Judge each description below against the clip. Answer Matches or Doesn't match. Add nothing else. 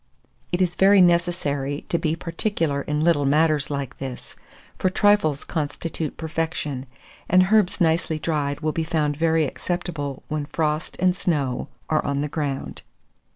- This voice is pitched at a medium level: Matches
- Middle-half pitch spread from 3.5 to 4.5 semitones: Doesn't match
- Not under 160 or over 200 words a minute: Doesn't match